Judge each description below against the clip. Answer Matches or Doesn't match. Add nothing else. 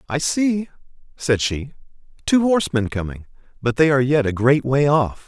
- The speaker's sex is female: Doesn't match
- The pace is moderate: Matches